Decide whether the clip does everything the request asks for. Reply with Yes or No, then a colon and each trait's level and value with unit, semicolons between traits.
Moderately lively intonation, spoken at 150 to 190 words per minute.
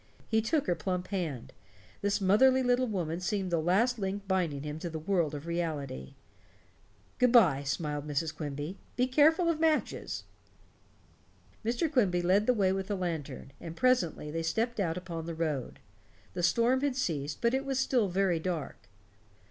No: wide, 6.6 semitones; average, 170 wpm